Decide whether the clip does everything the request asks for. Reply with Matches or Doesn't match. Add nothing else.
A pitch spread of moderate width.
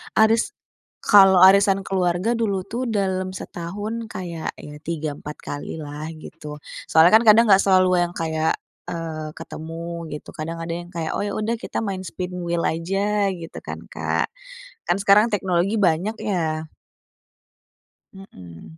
Matches